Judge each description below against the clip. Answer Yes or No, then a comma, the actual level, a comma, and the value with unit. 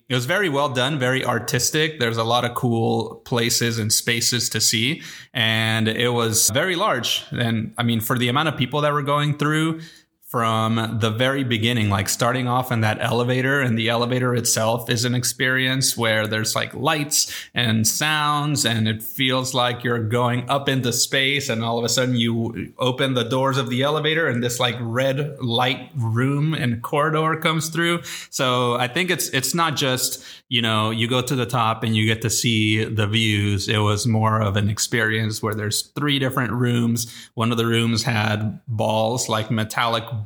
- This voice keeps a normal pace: Yes, average, 190 wpm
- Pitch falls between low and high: No, low, 120 Hz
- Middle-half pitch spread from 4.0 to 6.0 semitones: No, average, 2.8 semitones